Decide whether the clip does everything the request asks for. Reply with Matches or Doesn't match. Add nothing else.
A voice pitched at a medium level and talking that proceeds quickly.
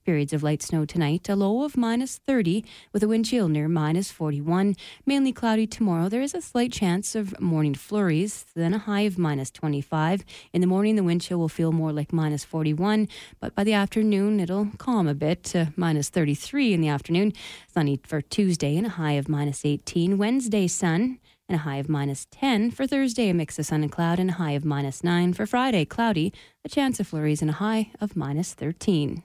Matches